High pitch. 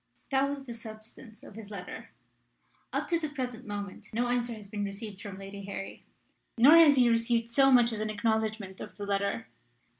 Yes: high, 225 Hz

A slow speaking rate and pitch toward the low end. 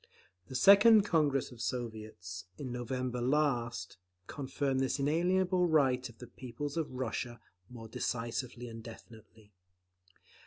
Yes: slow, 120 wpm; low, 125 Hz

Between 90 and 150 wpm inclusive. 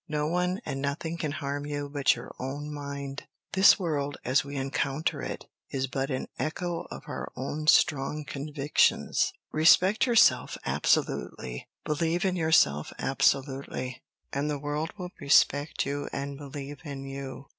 Yes: average, 145 wpm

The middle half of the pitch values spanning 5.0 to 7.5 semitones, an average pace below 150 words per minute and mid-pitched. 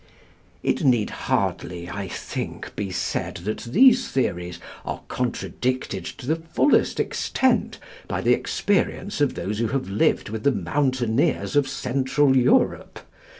No: wide, 5.4 semitones; slow, 135 wpm; low, 130 Hz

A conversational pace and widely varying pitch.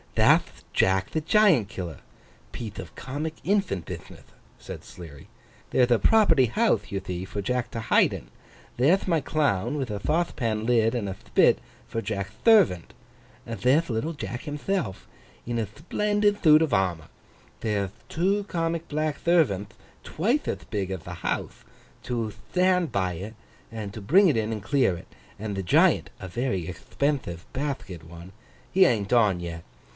Yes: average, 160 wpm; wide, 8.3 semitones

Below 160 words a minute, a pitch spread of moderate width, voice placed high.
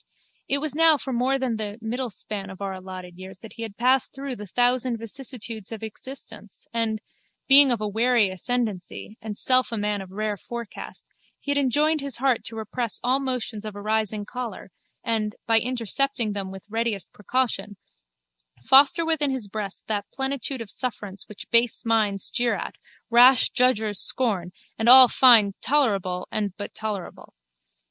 No: average, 170 wpm; average, 3.8 semitones; high, 225 Hz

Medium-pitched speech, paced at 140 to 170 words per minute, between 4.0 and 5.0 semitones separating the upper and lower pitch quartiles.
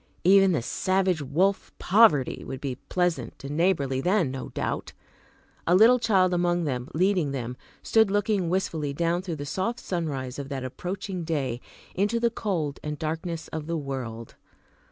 No: medium, 170 Hz; average, 160 wpm; wide, 5.4 semitones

